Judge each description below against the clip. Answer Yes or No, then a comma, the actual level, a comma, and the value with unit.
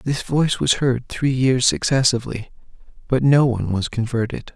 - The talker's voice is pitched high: No, low, 125 Hz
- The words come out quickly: No, average, 160 wpm